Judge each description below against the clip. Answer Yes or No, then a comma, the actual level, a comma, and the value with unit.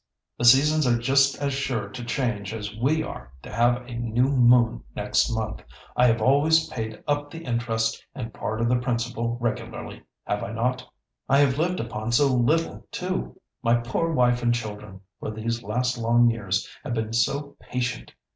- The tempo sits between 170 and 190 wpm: Yes, average, 180 wpm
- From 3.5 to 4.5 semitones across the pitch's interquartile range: No, average, 2.9 semitones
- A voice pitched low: Yes, low, 120 Hz